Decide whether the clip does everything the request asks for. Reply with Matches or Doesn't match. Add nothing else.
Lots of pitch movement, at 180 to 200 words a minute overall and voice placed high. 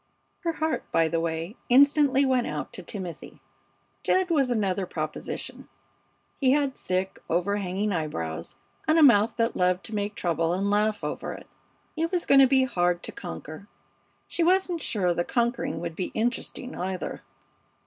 Doesn't match